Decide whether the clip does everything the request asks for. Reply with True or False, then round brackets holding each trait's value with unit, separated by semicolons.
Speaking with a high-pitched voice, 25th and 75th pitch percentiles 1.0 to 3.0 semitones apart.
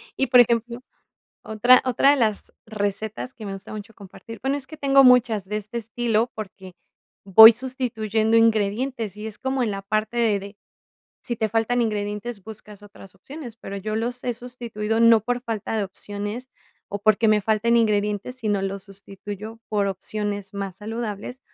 True (220 Hz; 2.7 semitones)